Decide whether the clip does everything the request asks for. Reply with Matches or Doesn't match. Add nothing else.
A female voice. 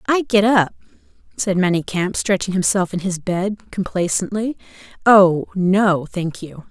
Matches